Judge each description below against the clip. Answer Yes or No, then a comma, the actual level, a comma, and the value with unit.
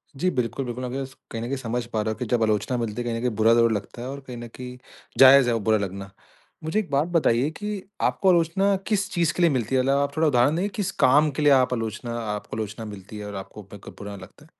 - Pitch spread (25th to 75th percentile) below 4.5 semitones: No, average, 4.8 semitones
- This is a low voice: Yes, low, 125 Hz